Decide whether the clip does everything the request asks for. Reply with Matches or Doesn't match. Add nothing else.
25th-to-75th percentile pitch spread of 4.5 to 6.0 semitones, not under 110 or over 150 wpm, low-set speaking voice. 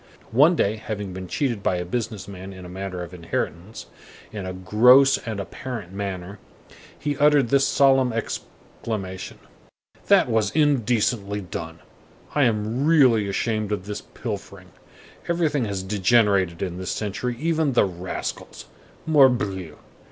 Matches